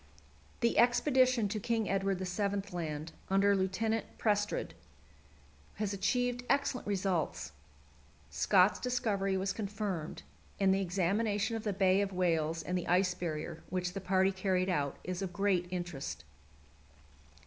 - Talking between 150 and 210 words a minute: No, slow, 135 wpm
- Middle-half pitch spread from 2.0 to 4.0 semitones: Yes, narrow, 2.6 semitones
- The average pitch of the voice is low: No, high, 195 Hz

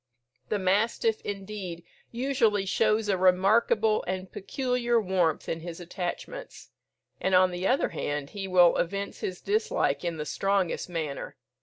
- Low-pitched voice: No, high, 190 Hz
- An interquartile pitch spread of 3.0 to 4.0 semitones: Yes, average, 3.4 semitones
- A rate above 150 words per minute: No, average, 140 wpm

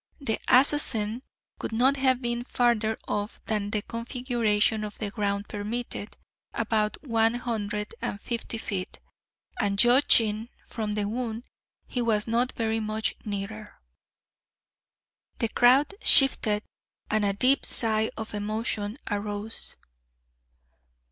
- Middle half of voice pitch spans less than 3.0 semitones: Yes, narrow, 2.4 semitones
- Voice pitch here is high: Yes, high, 220 Hz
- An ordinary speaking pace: No, slow, 120 wpm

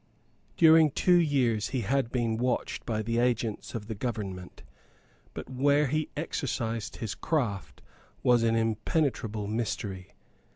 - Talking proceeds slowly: Yes, slow, 130 wpm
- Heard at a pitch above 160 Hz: No, low, 115 Hz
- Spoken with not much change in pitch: No, average, 4.2 semitones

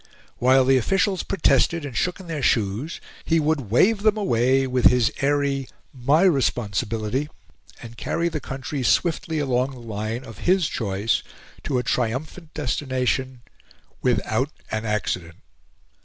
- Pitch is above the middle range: No, low, 130 Hz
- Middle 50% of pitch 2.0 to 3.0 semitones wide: No, average, 4.9 semitones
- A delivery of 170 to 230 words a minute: No, average, 140 wpm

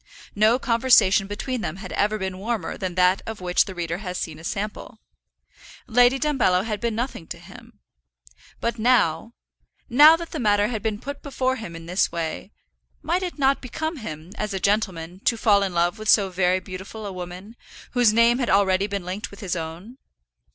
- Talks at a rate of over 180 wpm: Yes, average, 195 wpm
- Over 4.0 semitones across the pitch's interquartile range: Yes, average, 4.5 semitones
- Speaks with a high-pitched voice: Yes, high, 205 Hz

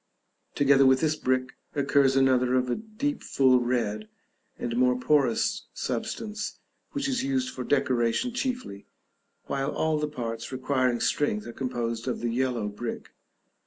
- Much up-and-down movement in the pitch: No, average, 4.0 semitones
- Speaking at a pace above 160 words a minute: No, average, 145 wpm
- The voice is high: No, low, 130 Hz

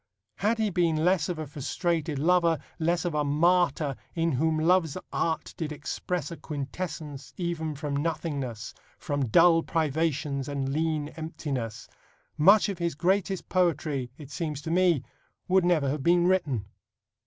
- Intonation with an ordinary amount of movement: Yes, average, 3.3 semitones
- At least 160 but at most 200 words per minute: No, average, 150 wpm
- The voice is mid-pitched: Yes, medium, 160 Hz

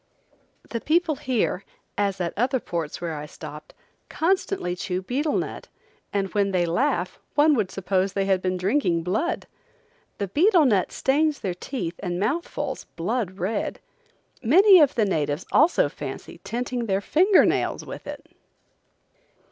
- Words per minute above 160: No, average, 150 wpm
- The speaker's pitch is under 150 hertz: No, high, 205 Hz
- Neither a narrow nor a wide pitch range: No, wide, 7.9 semitones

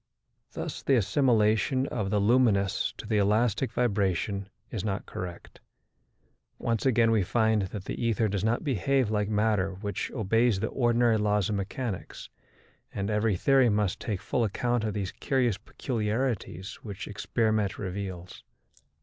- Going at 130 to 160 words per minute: Yes, average, 145 wpm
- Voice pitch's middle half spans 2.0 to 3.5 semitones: Yes, average, 3.0 semitones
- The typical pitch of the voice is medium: No, low, 105 Hz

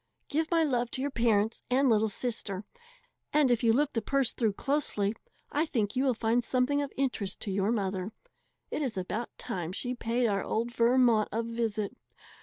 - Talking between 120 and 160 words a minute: No, average, 190 wpm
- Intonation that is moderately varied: Yes, average, 3.6 semitones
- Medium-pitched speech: No, high, 235 Hz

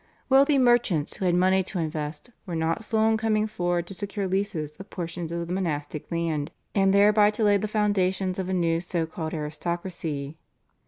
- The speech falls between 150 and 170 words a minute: No, average, 190 wpm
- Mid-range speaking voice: Yes, medium, 180 Hz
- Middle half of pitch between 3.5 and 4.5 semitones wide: Yes, average, 3.8 semitones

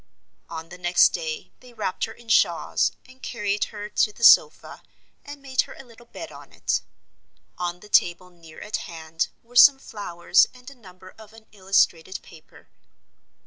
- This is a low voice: No, high, 205 Hz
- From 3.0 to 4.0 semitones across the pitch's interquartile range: No, average, 5.1 semitones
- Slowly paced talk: No, average, 180 wpm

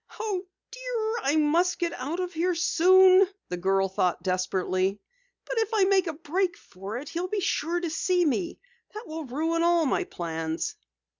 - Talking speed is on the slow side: No, average, 175 wpm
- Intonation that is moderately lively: No, wide, 8.4 semitones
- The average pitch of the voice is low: No, very high, 335 Hz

